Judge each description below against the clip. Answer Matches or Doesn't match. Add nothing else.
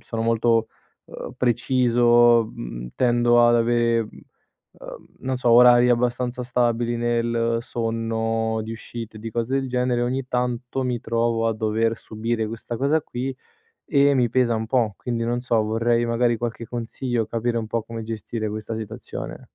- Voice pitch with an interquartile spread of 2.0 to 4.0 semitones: Doesn't match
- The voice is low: Matches